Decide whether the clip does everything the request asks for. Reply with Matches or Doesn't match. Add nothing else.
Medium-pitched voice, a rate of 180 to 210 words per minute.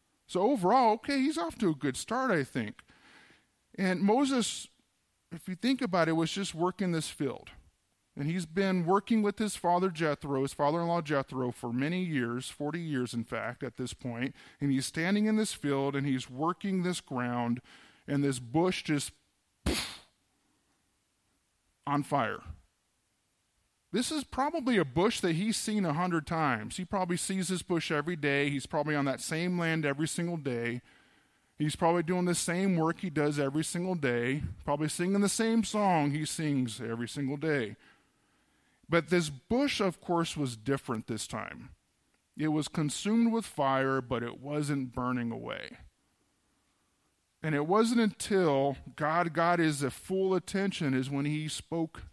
Doesn't match